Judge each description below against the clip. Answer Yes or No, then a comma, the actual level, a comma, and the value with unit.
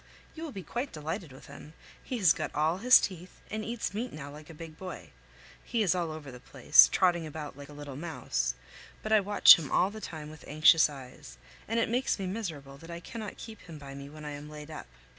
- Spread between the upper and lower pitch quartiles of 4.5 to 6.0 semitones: Yes, wide, 5.5 semitones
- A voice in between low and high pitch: Yes, medium, 160 Hz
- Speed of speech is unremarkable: No, fast, 235 wpm